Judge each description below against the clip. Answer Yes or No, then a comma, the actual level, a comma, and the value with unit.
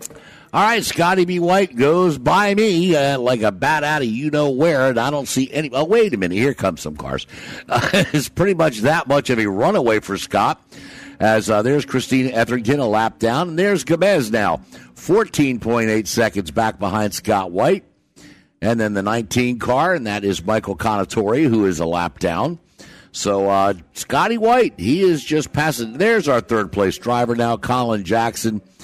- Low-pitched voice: Yes, low, 125 Hz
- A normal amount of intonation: No, wide, 6.5 semitones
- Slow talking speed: No, average, 185 wpm